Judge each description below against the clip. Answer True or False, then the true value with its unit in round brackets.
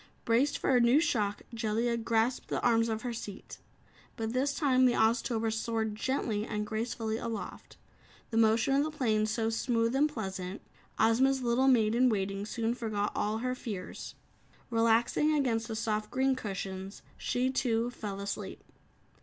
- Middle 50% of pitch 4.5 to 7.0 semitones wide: False (2.6 semitones)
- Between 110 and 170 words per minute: True (160 wpm)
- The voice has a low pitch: False (230 Hz)